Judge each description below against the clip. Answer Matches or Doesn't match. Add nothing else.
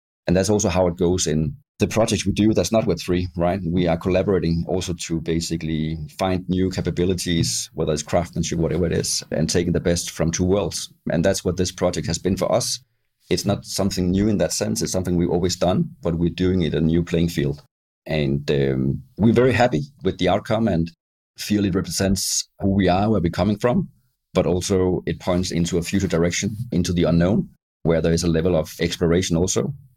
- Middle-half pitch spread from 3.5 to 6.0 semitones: Doesn't match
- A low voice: Matches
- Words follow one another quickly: Matches